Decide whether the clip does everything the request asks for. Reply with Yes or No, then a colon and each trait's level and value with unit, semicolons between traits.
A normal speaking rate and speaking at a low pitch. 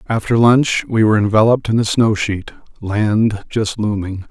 Yes: average, 165 wpm; low, 110 Hz